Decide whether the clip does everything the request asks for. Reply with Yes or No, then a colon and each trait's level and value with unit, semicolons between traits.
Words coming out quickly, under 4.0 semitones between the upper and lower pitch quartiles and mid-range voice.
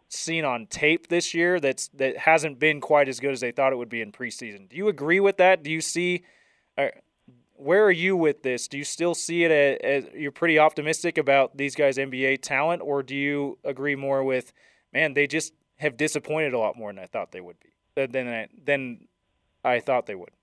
Yes: fast, 225 wpm; average, 3.2 semitones; medium, 150 Hz